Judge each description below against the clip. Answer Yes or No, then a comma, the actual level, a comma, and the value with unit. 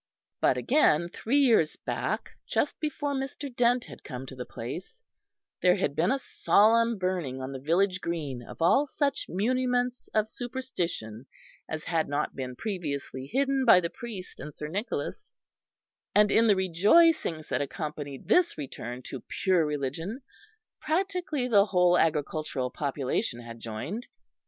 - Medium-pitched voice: Yes, medium, 180 Hz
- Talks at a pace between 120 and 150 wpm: Yes, average, 145 wpm